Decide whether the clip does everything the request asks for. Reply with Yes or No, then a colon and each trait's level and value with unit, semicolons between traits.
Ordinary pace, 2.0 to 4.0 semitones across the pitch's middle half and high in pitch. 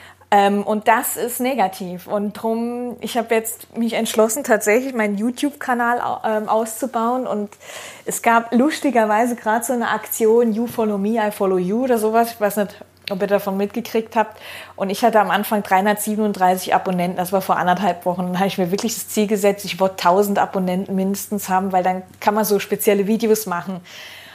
Yes: average, 180 wpm; average, 2.7 semitones; high, 215 Hz